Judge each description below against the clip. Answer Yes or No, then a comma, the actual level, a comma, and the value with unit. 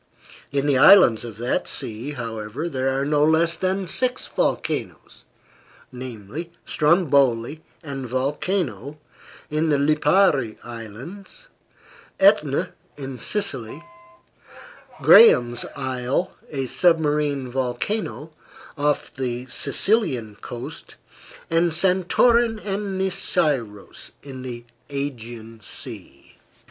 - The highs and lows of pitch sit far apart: Yes, wide, 5.7 semitones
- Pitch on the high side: No, medium, 140 Hz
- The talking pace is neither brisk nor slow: No, slow, 95 wpm